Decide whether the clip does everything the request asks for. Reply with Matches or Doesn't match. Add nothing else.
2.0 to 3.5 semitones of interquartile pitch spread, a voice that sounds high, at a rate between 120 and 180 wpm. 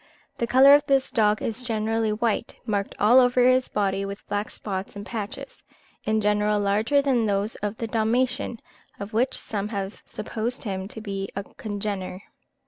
Matches